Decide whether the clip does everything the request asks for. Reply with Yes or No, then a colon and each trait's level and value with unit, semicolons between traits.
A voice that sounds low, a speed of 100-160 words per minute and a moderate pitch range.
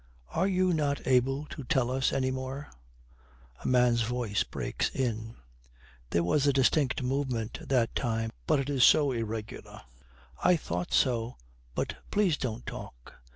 Yes: low, 130 Hz; average, 150 wpm; average, 3.6 semitones